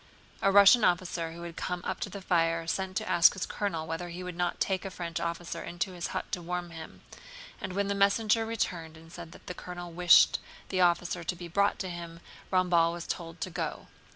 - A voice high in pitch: No, medium, 175 Hz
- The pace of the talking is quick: Yes, fast, 220 wpm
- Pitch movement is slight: Yes, narrow, 1.9 semitones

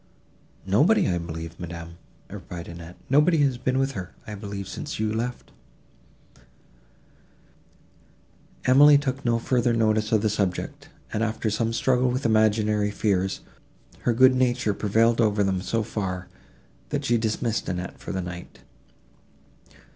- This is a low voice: Yes, low, 110 Hz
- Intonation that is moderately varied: Yes, average, 4.3 semitones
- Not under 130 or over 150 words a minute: Yes, average, 140 wpm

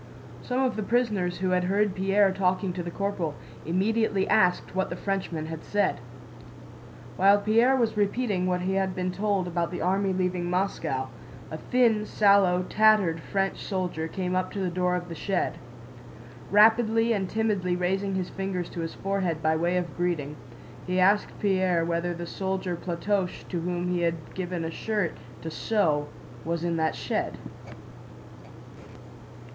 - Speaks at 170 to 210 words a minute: No, average, 160 wpm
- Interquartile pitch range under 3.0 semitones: Yes, narrow, 2.5 semitones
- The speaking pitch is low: No, medium, 185 Hz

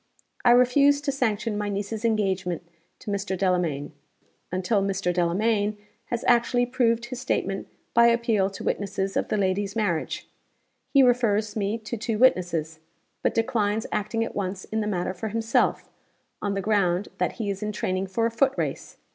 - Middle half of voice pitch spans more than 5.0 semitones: No, average, 3.2 semitones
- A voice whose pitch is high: Yes, high, 210 Hz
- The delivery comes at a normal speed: Yes, average, 170 wpm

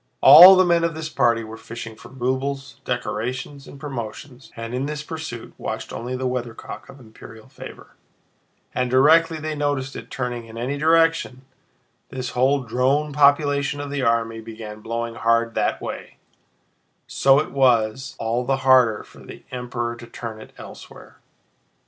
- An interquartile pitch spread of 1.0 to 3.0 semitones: No, average, 3.5 semitones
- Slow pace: No, average, 160 wpm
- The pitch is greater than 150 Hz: No, low, 130 Hz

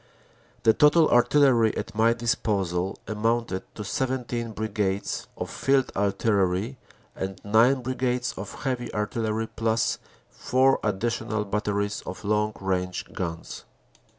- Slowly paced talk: Yes, slow, 115 wpm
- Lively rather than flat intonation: No, average, 3.1 semitones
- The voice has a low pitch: Yes, low, 110 Hz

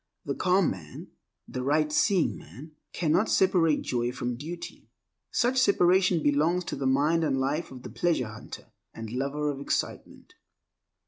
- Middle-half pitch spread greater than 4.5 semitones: Yes, average, 4.9 semitones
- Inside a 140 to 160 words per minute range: Yes, average, 150 wpm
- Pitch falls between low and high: Yes, medium, 150 Hz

